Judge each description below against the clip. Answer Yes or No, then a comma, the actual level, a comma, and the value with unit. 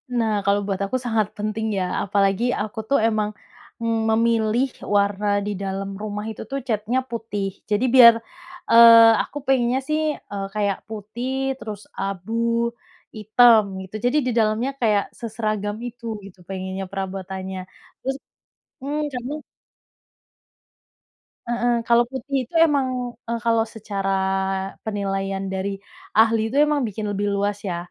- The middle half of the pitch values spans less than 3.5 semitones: Yes, average, 2.9 semitones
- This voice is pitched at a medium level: No, high, 215 Hz